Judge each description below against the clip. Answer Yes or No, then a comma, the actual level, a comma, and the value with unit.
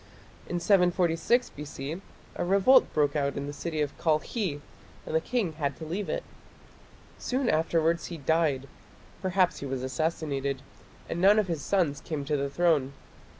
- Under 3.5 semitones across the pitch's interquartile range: No, average, 4.1 semitones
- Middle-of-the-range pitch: Yes, medium, 160 Hz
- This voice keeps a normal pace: Yes, average, 160 wpm